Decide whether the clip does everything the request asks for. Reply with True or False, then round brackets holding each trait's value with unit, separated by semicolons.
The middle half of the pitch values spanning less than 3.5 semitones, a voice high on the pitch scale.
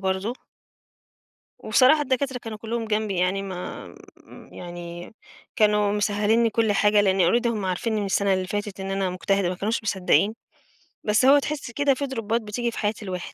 True (3.1 semitones; 210 Hz)